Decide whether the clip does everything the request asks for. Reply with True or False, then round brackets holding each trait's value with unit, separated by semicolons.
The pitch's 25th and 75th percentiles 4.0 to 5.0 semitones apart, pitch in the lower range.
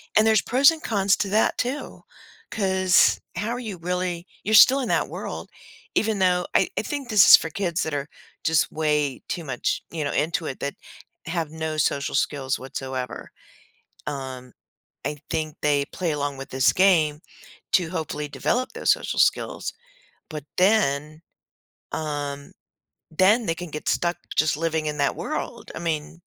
False (4.5 semitones; 160 Hz)